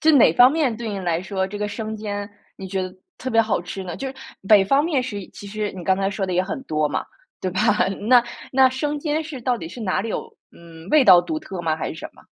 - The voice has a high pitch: Yes, high, 205 Hz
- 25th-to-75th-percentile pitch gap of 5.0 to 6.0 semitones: Yes, wide, 5.5 semitones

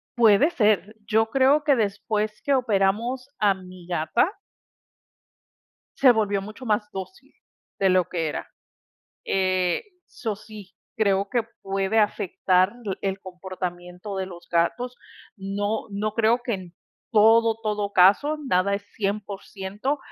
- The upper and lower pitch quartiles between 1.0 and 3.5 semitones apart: Yes, average, 2.9 semitones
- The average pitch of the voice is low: No, high, 205 Hz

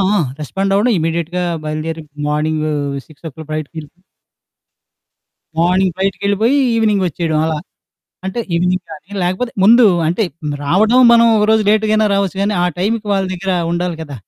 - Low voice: No, medium, 180 Hz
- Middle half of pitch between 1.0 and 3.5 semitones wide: No, average, 4.6 semitones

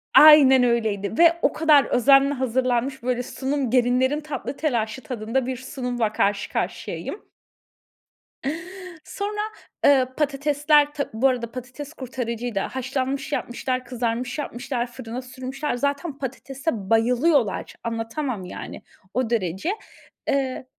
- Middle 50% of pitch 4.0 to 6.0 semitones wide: No, average, 3.0 semitones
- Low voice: No, very high, 255 Hz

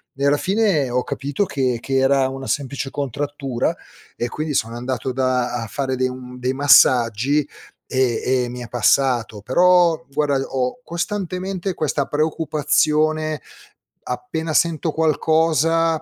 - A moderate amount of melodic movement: Yes, average, 3.7 semitones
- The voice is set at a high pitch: No, medium, 140 Hz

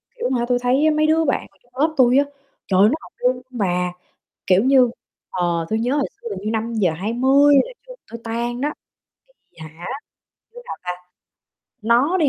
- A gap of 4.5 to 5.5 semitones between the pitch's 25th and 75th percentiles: Yes, average, 5.1 semitones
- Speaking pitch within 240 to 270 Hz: Yes, high, 245 Hz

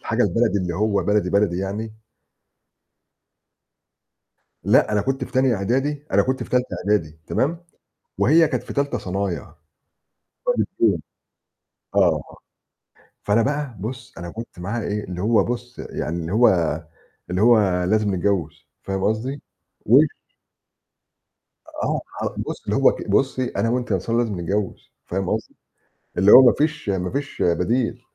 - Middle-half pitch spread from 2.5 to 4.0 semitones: No, average, 4.9 semitones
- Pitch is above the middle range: No, low, 105 Hz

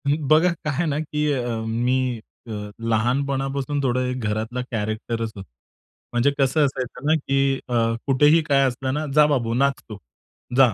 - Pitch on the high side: No, low, 130 Hz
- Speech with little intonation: No, average, 3.2 semitones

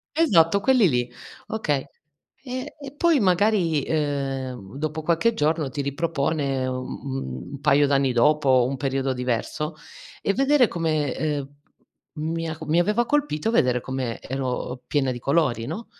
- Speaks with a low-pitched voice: No, medium, 150 Hz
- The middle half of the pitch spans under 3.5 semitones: No, average, 4.7 semitones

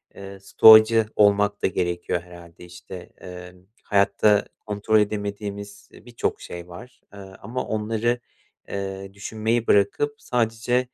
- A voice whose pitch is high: No, low, 100 Hz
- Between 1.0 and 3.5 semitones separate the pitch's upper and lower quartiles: Yes, narrow, 2.5 semitones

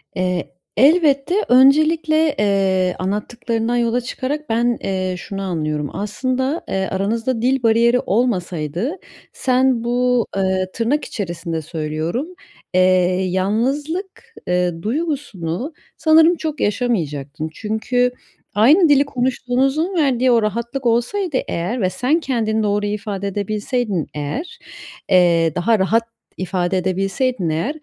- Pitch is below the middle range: No, high, 230 Hz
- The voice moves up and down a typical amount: No, wide, 5.9 semitones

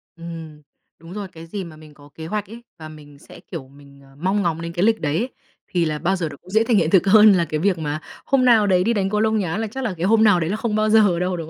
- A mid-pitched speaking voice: Yes, medium, 180 Hz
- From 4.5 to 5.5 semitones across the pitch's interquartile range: Yes, average, 4.8 semitones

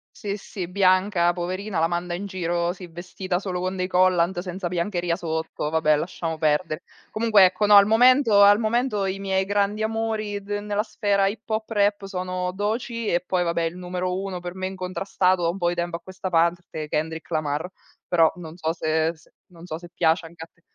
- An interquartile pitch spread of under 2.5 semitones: No, average, 2.8 semitones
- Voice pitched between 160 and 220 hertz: Yes, medium, 185 Hz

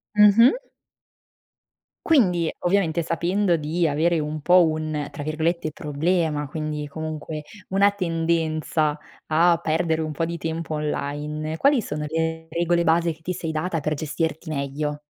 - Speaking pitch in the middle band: Yes, medium, 160 Hz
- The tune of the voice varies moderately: No, narrow, 2.0 semitones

